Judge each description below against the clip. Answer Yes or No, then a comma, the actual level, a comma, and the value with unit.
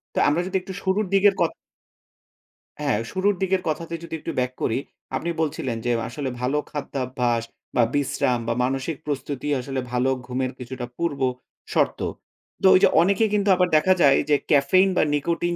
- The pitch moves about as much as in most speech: No, wide, 5.9 semitones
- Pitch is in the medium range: Yes, medium, 145 Hz